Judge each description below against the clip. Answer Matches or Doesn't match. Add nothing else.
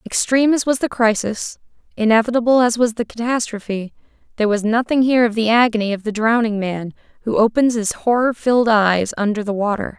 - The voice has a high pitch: Matches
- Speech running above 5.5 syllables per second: Matches